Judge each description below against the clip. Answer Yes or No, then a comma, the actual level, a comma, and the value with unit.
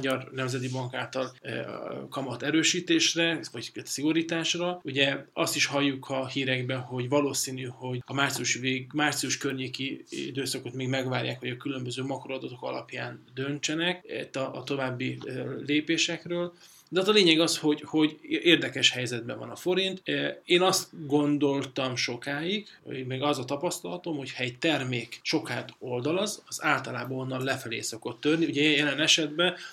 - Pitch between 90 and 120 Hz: No, medium, 140 Hz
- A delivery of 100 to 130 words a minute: No, average, 140 wpm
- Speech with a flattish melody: No, average, 3.7 semitones